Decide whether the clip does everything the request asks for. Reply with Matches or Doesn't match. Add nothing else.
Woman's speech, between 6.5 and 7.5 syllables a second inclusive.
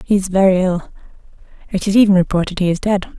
Matches